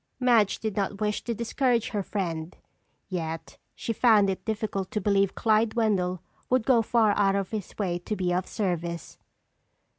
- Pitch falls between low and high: No, high, 205 Hz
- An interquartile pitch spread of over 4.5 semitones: No, average, 3.2 semitones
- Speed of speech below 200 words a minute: Yes, average, 170 wpm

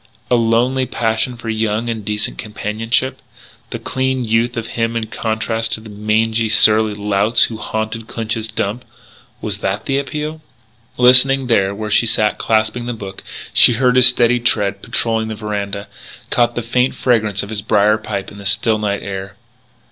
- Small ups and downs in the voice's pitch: Yes, narrow, 2.2 semitones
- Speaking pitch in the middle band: No, low, 110 Hz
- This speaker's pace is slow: No, average, 170 wpm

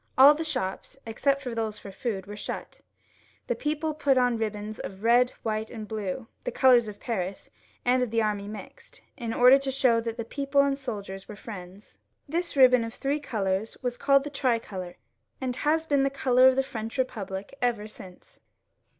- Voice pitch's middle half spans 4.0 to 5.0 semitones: Yes, average, 4.3 semitones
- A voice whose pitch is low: No, high, 235 Hz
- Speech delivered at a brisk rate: No, average, 190 wpm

